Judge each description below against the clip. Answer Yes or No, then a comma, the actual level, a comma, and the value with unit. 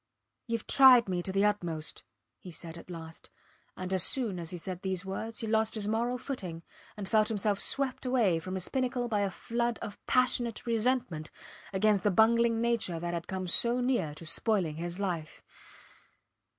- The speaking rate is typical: Yes, average, 180 wpm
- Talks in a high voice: Yes, high, 205 Hz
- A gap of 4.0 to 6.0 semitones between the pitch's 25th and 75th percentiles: Yes, average, 4.9 semitones